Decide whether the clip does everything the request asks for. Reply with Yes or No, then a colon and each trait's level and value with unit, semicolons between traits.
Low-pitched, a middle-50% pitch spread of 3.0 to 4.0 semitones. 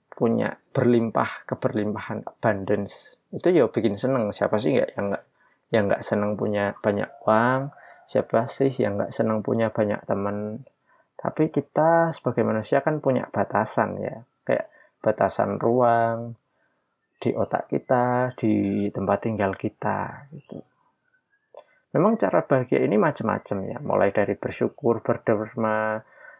Yes: low, 115 Hz; average, 3.6 semitones